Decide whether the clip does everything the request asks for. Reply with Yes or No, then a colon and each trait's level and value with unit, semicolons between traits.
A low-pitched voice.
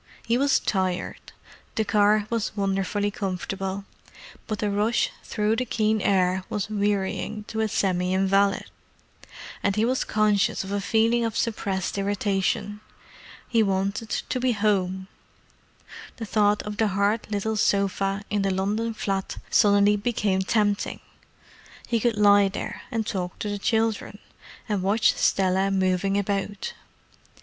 No: high, 205 Hz